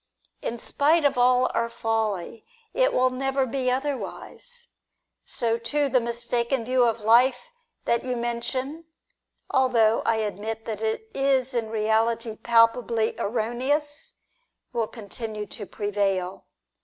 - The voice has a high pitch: Yes, high, 235 Hz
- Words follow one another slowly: Yes, slow, 125 wpm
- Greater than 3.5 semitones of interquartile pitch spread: No, average, 2.8 semitones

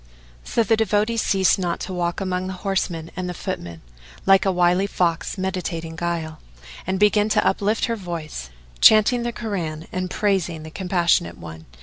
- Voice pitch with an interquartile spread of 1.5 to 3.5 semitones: Yes, average, 3.1 semitones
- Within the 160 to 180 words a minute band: Yes, average, 175 wpm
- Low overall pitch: No, medium, 185 Hz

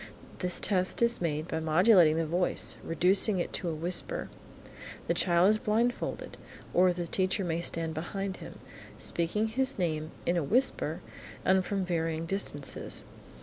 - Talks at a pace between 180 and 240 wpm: No, average, 150 wpm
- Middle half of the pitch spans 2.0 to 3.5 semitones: Yes, average, 3.1 semitones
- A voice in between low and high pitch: Yes, medium, 180 Hz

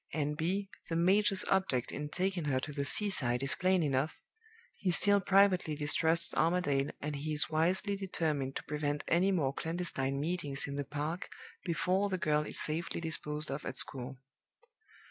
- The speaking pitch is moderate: Yes, medium, 155 Hz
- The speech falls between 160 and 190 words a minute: Yes, average, 165 wpm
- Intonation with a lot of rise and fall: No, average, 4.2 semitones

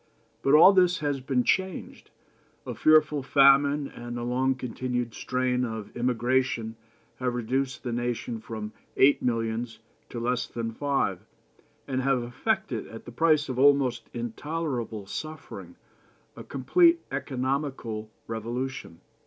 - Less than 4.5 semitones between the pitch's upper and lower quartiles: Yes, average, 2.9 semitones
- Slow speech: Yes, slow, 130 wpm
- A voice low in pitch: Yes, low, 125 Hz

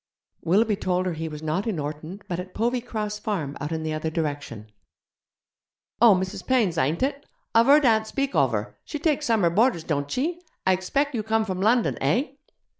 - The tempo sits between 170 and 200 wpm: Yes, average, 190 wpm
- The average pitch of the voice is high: Yes, high, 195 Hz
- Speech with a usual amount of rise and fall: No, wide, 6.7 semitones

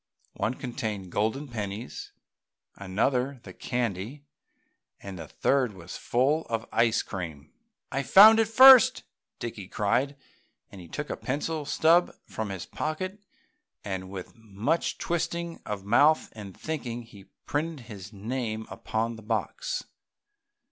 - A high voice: No, low, 115 Hz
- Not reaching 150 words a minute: Yes, slow, 135 wpm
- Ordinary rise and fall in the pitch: No, wide, 6.6 semitones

